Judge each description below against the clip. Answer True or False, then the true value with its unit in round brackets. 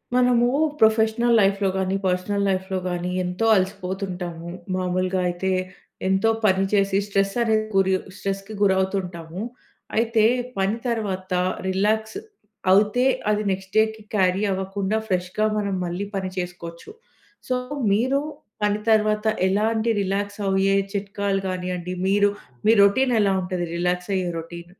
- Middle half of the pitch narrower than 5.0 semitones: True (2.4 semitones)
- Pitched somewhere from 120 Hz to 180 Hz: False (195 Hz)